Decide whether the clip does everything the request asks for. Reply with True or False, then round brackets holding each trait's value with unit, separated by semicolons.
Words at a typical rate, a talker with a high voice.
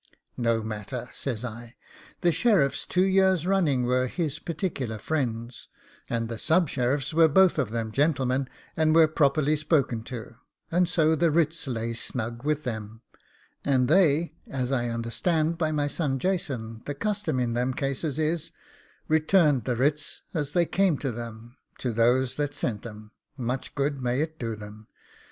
False (165 wpm; 135 Hz)